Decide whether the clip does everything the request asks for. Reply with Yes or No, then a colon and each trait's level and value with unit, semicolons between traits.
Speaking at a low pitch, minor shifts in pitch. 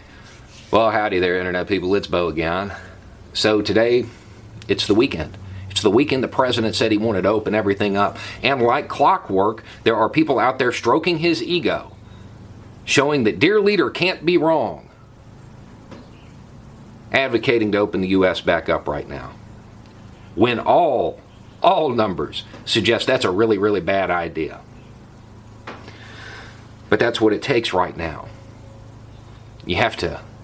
Yes: low, 110 Hz; narrow, 2.3 semitones